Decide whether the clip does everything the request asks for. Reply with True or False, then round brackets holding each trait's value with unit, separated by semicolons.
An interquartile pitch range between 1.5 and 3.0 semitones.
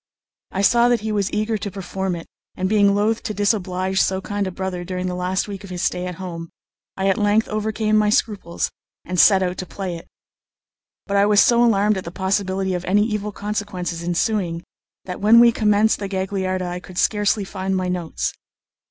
True (2.4 semitones)